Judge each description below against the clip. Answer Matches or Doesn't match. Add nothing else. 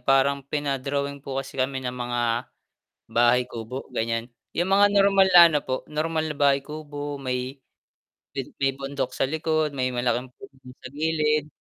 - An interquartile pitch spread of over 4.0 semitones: Doesn't match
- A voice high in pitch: Doesn't match